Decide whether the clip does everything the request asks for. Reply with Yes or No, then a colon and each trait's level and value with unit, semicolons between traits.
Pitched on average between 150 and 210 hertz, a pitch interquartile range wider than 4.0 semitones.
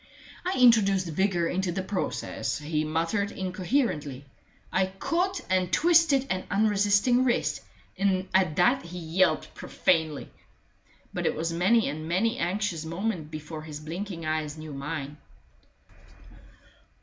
Yes: medium, 185 Hz; average, 4.4 semitones